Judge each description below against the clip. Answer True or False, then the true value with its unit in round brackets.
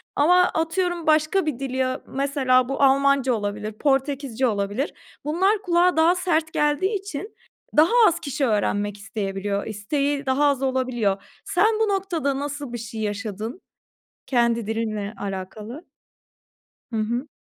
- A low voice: False (270 Hz)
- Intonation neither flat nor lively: False (6.1 semitones)